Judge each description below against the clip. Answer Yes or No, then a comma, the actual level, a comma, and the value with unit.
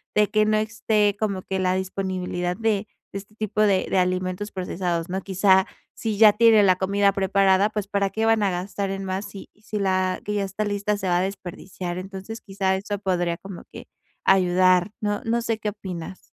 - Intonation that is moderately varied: No, narrow, 2.0 semitones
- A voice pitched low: No, high, 195 Hz